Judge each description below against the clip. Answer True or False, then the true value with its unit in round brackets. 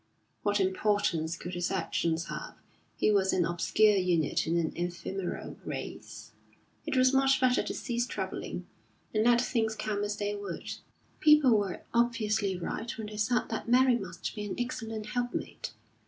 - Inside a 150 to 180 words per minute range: True (160 wpm)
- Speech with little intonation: False (4.4 semitones)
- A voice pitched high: True (210 Hz)